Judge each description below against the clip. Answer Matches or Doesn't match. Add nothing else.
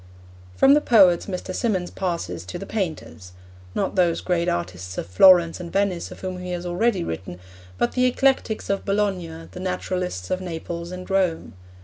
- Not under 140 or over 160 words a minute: Doesn't match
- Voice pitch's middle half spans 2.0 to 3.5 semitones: Matches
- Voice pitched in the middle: Matches